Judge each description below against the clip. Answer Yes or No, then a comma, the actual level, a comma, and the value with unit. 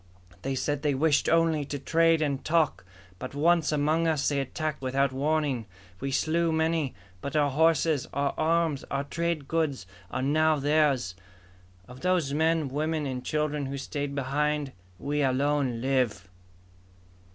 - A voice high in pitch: No, medium, 145 Hz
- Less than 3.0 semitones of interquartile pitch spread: Yes, narrow, 2.6 semitones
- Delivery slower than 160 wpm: Yes, average, 150 wpm